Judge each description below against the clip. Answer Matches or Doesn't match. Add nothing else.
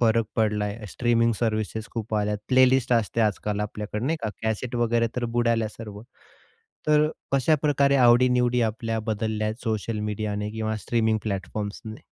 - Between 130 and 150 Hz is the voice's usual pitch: Doesn't match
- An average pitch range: Doesn't match